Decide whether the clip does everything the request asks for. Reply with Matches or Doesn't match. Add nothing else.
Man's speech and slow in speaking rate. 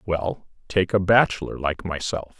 Matches